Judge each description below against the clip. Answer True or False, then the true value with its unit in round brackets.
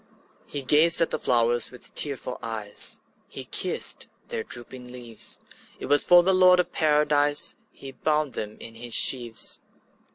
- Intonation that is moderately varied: True (4.2 semitones)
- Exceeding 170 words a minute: False (160 wpm)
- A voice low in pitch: True (130 Hz)